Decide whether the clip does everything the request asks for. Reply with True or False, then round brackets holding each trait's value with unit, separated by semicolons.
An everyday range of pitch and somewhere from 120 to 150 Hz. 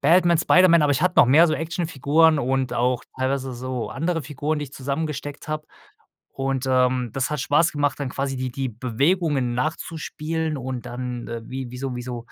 True (3.6 semitones; 135 Hz)